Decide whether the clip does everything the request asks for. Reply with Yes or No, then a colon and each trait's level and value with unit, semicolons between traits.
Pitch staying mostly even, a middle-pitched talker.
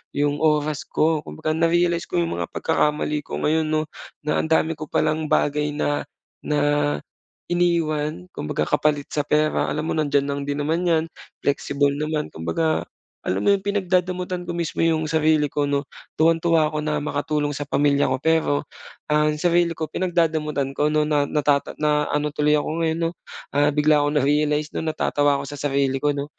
Yes: narrow, 1.7 semitones; medium, 150 Hz